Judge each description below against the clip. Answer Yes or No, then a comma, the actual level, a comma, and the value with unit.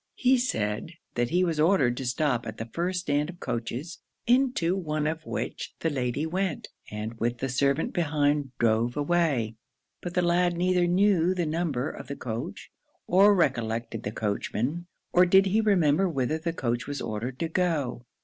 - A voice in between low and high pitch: Yes, medium, 155 Hz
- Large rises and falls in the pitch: Yes, wide, 6.4 semitones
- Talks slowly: No, average, 175 wpm